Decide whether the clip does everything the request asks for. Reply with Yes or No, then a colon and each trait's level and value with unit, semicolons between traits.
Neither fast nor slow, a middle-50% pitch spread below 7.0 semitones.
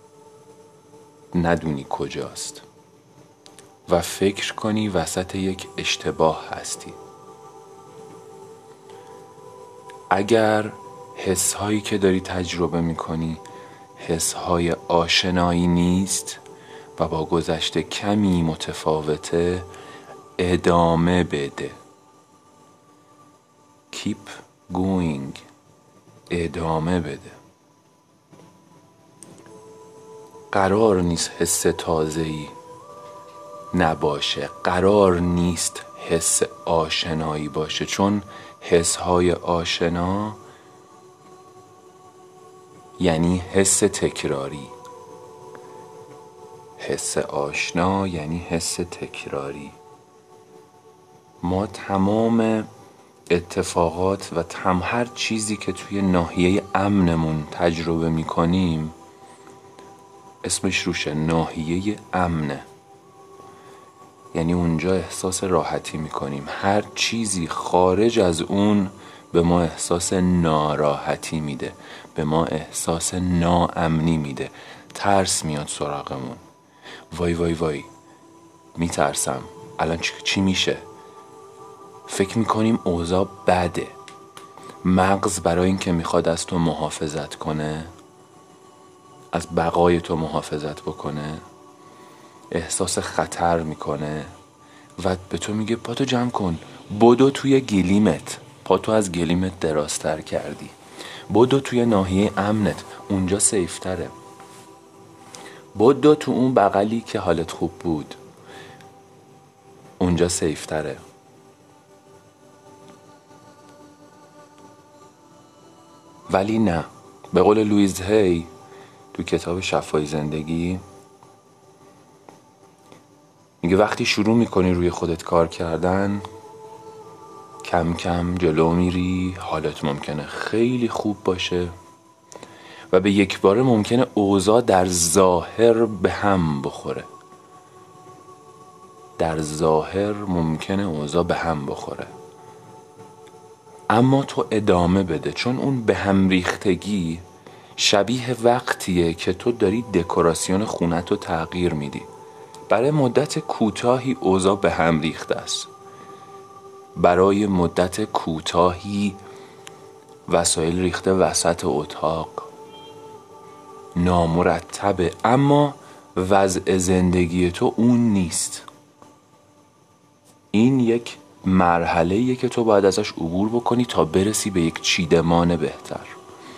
No: slow, 85 wpm; average, 5.1 semitones